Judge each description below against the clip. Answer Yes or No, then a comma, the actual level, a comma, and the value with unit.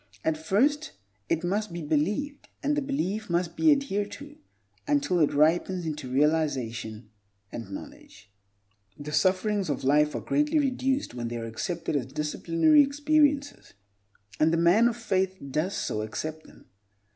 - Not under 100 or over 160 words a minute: Yes, average, 150 wpm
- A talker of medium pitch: Yes, medium, 175 Hz